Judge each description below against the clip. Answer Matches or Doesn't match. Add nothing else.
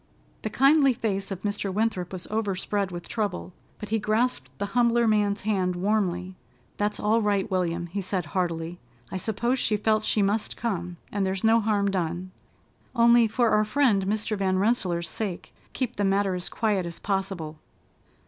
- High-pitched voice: Matches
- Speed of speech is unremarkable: Matches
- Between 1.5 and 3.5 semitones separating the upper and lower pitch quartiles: Matches